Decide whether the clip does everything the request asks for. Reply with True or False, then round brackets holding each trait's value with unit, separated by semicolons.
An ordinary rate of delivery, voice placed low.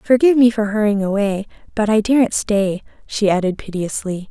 False (165 wpm; 210 Hz)